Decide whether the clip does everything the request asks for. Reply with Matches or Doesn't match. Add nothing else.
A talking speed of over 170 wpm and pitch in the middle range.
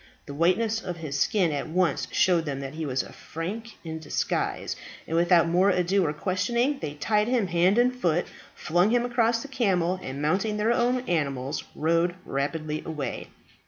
Matches